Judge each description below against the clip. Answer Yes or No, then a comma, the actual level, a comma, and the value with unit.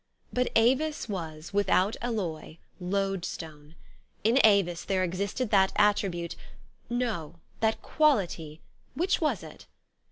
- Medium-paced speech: No, slow, 105 wpm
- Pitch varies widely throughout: No, average, 5.0 semitones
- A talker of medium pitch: No, high, 195 Hz